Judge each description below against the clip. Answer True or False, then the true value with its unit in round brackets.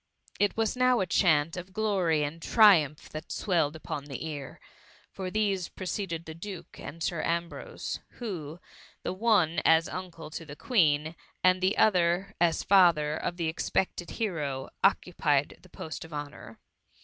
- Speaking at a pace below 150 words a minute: False (160 wpm)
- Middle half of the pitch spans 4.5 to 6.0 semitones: False (3.6 semitones)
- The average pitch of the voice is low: False (170 Hz)